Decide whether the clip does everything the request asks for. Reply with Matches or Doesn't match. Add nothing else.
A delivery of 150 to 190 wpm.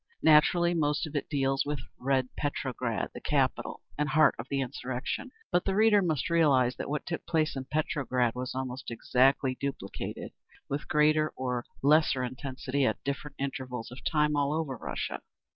Matches